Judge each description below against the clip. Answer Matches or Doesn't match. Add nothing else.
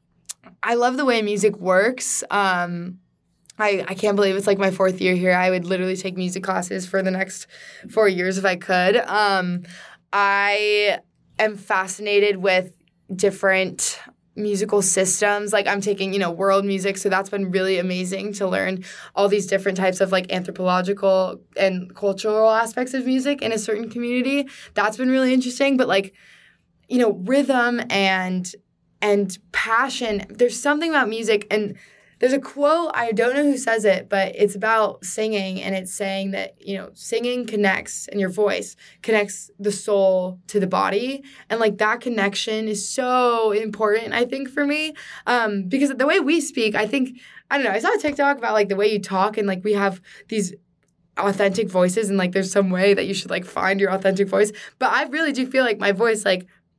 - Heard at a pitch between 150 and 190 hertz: Doesn't match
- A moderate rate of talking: Matches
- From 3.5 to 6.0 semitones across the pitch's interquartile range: Doesn't match